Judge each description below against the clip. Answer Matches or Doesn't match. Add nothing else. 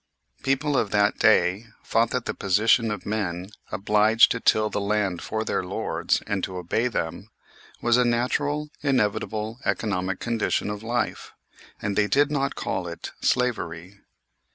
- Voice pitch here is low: Matches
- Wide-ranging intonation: Doesn't match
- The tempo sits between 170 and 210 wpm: Doesn't match